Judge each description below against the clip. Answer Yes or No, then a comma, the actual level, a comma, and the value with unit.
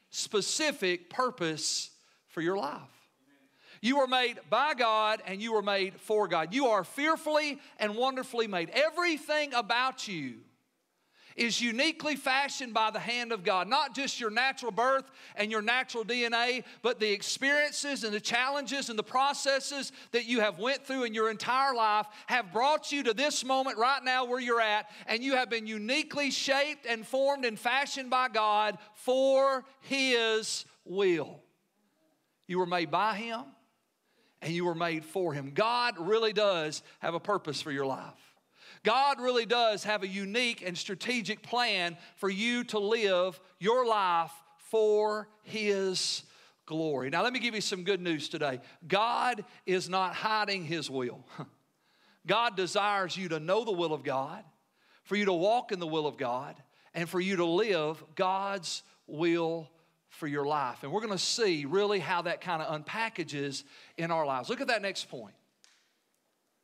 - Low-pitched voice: No, high, 215 Hz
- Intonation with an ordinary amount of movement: No, wide, 5.9 semitones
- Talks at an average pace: Yes, average, 165 wpm